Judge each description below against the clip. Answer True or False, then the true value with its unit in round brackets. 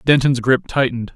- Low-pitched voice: True (130 Hz)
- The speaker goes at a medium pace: True (155 wpm)